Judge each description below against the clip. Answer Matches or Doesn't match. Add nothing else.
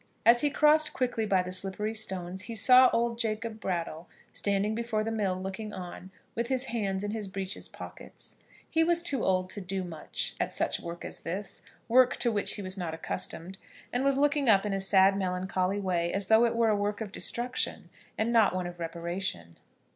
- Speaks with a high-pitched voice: Matches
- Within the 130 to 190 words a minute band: Doesn't match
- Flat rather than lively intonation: Doesn't match